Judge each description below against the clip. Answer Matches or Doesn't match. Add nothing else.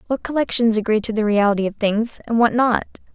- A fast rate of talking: Matches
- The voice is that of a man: Doesn't match